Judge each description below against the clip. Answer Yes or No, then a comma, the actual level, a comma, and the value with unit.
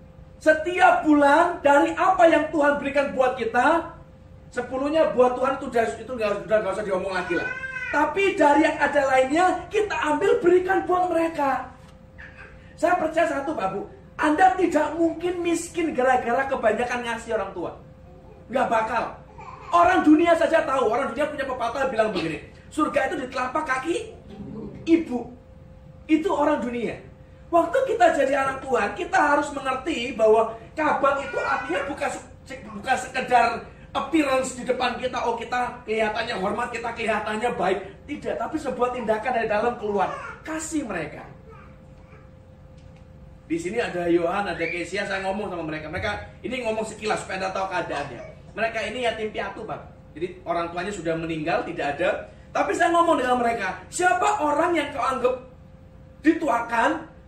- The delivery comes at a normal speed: No, fast, 150 wpm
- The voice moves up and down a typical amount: No, wide, 5.7 semitones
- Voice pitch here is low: No, very high, 265 Hz